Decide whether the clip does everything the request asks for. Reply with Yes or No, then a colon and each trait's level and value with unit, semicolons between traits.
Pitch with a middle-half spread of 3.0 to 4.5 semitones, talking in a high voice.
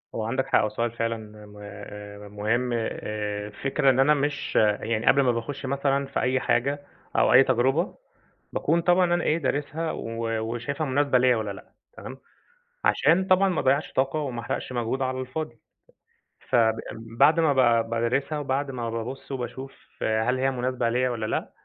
No: average, 3.4 semitones; low, 130 Hz